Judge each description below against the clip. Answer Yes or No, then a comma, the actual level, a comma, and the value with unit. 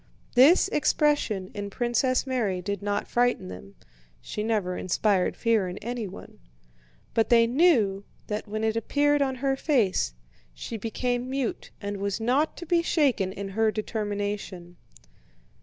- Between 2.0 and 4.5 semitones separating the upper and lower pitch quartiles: Yes, average, 4.2 semitones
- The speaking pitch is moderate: No, high, 220 Hz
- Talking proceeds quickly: No, average, 140 wpm